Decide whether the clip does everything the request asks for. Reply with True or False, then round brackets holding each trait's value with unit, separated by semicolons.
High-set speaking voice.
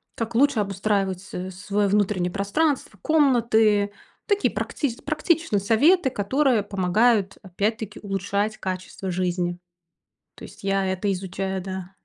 True (200 Hz)